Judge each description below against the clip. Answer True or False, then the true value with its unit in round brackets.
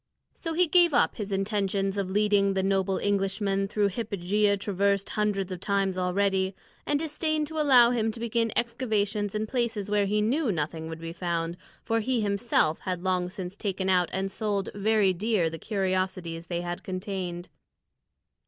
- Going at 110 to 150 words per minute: False (170 wpm)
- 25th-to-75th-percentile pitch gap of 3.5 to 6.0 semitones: False (2.7 semitones)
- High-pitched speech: True (200 Hz)